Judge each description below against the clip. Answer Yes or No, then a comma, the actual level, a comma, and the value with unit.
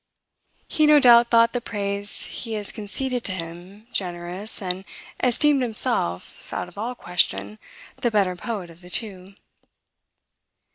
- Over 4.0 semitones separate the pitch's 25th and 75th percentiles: Yes, average, 4.8 semitones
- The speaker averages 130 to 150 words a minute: Yes, average, 140 wpm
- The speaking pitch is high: Yes, high, 205 Hz